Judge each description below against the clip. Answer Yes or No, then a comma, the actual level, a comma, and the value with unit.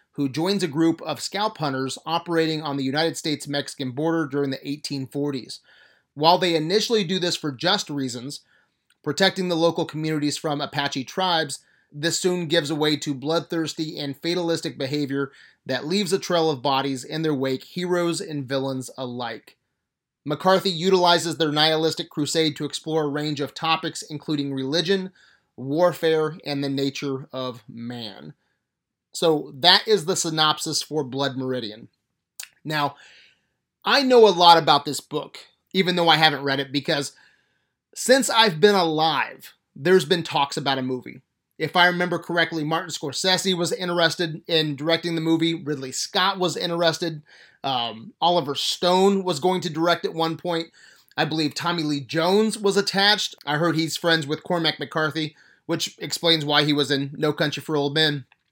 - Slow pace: No, average, 160 wpm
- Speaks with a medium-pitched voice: Yes, medium, 160 Hz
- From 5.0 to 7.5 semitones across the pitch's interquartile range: No, average, 3.2 semitones